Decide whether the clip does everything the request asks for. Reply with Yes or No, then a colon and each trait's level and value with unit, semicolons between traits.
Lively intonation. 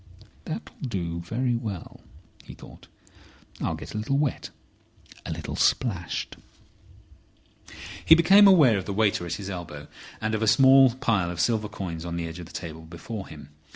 Yes: wide, 6.0 semitones